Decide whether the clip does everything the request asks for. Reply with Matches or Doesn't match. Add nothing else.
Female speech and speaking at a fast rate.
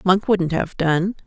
Doesn't match